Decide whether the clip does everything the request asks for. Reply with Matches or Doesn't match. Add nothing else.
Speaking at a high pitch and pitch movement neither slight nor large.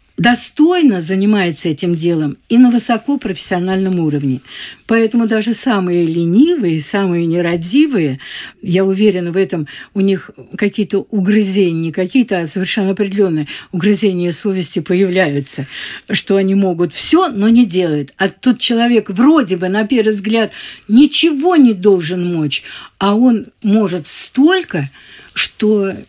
Matches